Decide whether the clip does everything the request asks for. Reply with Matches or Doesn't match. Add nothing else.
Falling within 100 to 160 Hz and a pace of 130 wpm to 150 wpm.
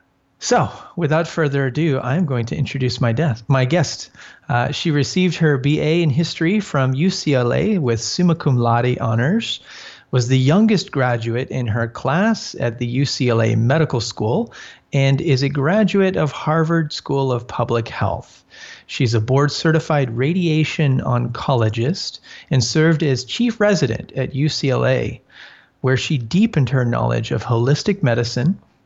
Matches